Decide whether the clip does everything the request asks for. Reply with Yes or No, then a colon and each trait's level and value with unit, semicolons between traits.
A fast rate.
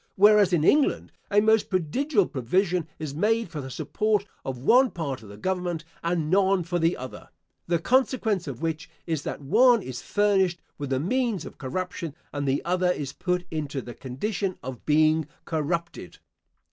No: average, 175 wpm